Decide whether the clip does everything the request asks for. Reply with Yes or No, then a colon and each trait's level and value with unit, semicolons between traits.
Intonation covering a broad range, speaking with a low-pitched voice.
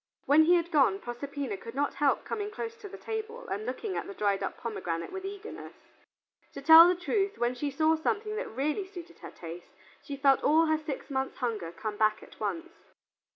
No: wide, 7.8 semitones; very high, 300 Hz